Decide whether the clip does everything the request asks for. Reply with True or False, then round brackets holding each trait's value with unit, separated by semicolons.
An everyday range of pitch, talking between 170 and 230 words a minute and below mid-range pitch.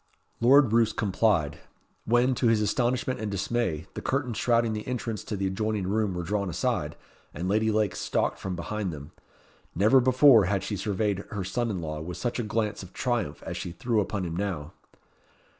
True (3.9 semitones; 190 wpm; 105 Hz)